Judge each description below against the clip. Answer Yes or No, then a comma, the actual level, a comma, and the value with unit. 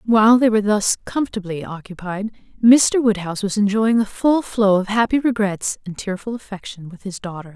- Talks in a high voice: Yes, high, 210 Hz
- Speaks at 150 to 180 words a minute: Yes, average, 175 wpm